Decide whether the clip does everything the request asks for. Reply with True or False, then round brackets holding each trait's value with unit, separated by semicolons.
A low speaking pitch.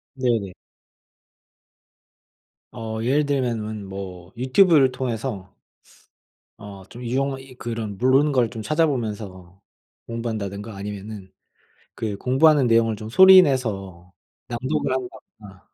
True (115 Hz)